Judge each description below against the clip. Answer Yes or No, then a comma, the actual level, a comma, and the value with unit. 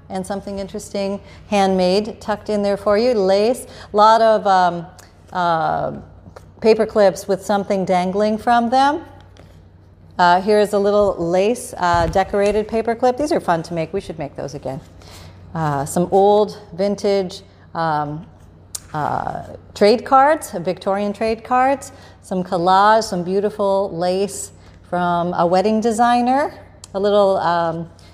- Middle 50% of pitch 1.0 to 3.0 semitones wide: No, average, 3.4 semitones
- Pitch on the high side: Yes, high, 195 Hz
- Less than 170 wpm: Yes, average, 140 wpm